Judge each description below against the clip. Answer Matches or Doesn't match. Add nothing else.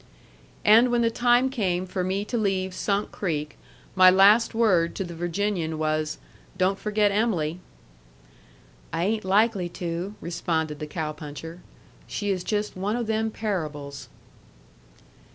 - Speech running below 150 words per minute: Matches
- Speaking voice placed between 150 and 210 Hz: Matches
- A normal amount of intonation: Matches